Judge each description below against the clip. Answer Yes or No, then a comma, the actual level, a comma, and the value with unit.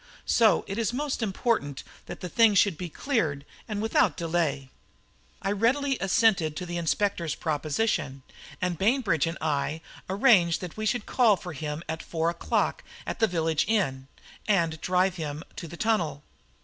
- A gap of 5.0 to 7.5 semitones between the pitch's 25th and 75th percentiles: Yes, wide, 5.4 semitones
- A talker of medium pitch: Yes, medium, 180 Hz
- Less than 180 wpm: Yes, average, 160 wpm